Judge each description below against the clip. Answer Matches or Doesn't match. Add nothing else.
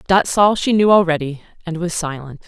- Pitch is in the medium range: Matches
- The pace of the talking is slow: Doesn't match